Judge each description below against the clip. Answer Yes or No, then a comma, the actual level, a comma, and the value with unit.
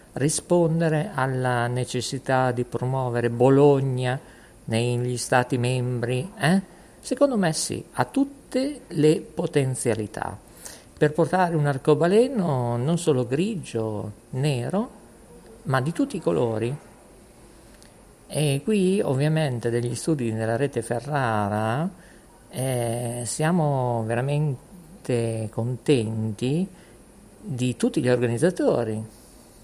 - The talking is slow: Yes, slow, 95 wpm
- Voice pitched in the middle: No, low, 130 Hz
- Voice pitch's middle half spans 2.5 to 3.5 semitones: No, average, 5.3 semitones